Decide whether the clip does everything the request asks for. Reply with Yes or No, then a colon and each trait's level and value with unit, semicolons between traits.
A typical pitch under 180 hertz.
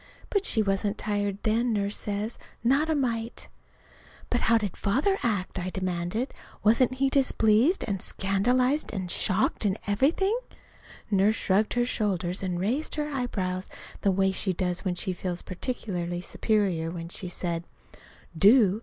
No: high, 205 Hz